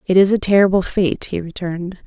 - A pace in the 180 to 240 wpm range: Yes, fast, 205 wpm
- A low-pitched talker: No, medium, 185 Hz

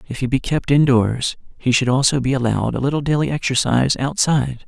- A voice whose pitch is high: No, low, 130 Hz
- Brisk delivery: No, average, 195 wpm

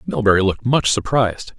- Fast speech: No, average, 150 wpm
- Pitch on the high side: No, low, 110 Hz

